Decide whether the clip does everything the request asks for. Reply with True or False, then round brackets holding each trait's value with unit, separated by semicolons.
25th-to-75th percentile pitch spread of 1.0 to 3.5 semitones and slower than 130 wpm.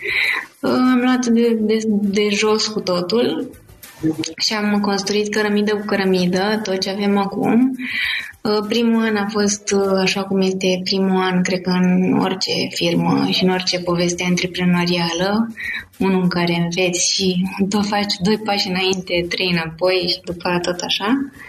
False (2.8 semitones; 150 wpm)